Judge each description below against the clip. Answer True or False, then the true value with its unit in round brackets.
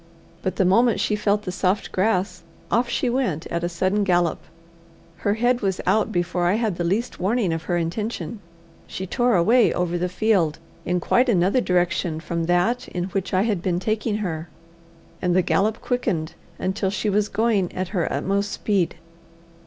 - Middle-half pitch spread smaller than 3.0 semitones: False (3.6 semitones)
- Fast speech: False (180 wpm)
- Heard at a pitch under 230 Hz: True (190 Hz)